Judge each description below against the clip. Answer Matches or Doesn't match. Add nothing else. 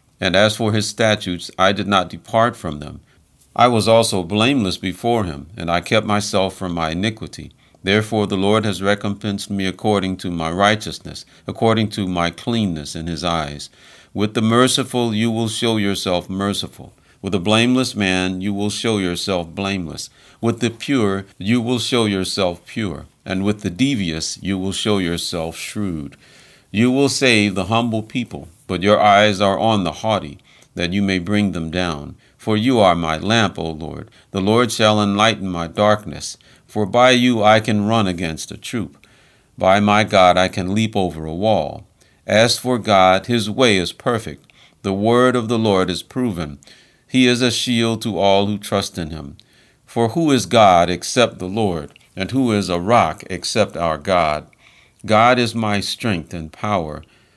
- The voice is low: Matches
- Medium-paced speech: Matches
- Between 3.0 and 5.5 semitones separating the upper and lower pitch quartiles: Matches